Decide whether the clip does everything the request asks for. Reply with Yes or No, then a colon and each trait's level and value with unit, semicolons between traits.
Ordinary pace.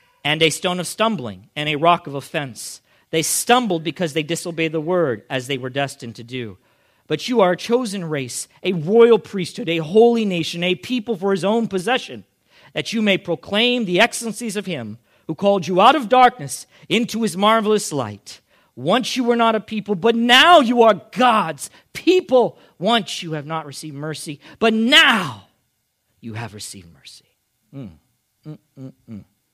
Yes: average, 170 wpm